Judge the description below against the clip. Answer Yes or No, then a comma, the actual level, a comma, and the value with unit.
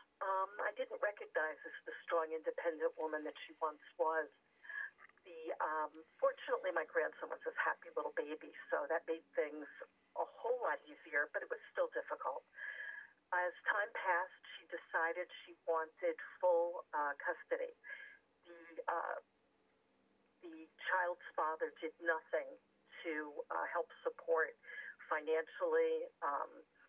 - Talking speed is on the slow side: Yes, slow, 130 wpm